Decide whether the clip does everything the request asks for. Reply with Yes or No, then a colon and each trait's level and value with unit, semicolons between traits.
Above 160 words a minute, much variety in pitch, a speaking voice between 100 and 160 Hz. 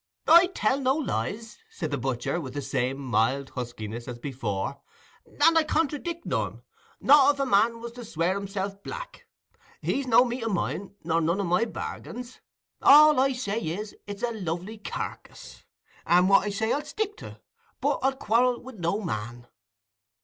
No: average, 170 wpm; wide, 8.7 semitones; high, 205 Hz